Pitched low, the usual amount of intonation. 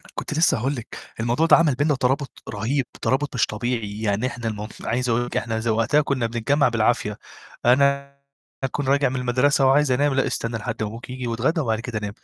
Yes: low, 125 Hz; average, 3.5 semitones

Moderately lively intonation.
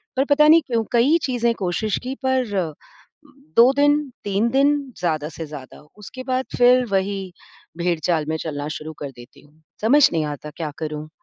No: wide, 8.6 semitones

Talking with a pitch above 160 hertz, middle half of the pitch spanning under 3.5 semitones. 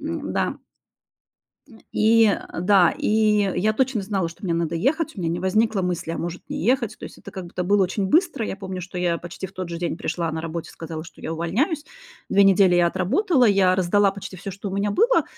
No: high, 190 Hz; average, 3.8 semitones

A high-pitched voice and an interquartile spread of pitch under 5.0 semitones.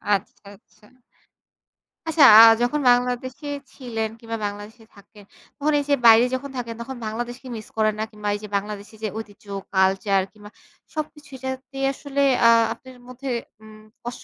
Yes: high, 230 Hz; average, 3.7 semitones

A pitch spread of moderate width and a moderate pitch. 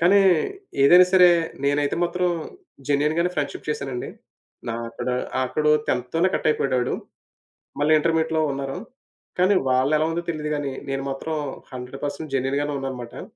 Yes: average, 3.2 semitones; medium, 145 Hz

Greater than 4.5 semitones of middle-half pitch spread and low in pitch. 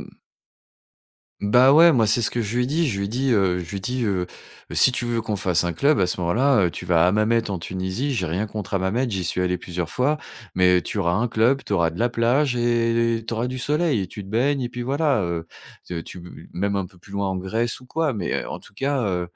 Yes: average, 5.2 semitones; low, 110 Hz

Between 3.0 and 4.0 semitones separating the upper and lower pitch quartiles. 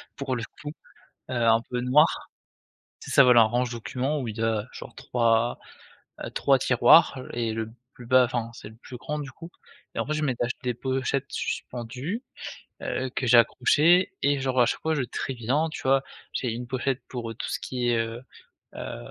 No: narrow, 2.6 semitones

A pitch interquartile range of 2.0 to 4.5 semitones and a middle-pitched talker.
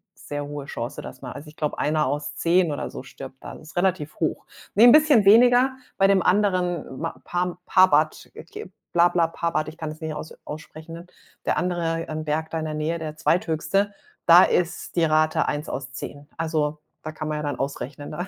Yes: average, 2.8 semitones; medium, 160 Hz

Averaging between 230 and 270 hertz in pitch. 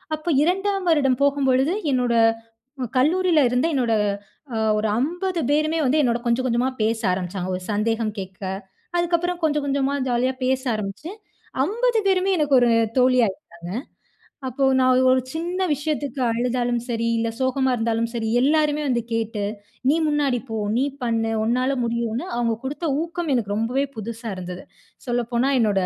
Yes: very high, 255 Hz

